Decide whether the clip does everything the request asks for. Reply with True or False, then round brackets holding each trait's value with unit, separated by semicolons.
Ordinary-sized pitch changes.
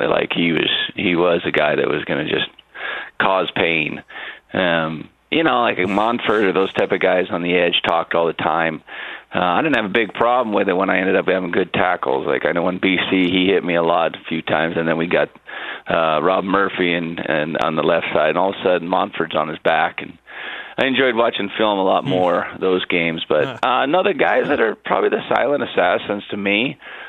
True (3.0 semitones)